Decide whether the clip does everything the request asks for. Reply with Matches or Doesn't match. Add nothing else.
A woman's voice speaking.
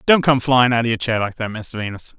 Doesn't match